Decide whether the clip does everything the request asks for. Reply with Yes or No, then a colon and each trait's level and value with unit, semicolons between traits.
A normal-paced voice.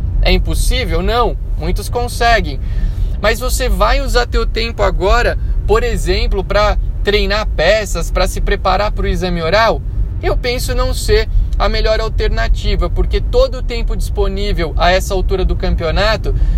Yes: average, 150 wpm